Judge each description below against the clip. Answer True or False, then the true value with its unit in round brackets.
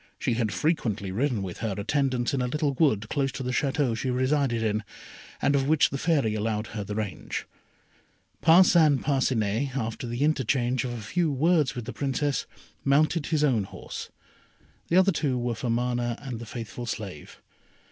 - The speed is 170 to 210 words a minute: True (180 wpm)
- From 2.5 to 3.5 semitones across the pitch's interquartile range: False (4.1 semitones)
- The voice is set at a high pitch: False (125 Hz)